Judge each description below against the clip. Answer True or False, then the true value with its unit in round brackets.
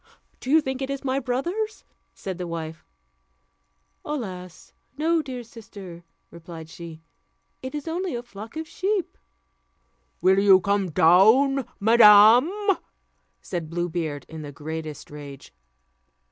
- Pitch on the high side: True (205 Hz)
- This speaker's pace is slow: True (130 wpm)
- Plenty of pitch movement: True (8.1 semitones)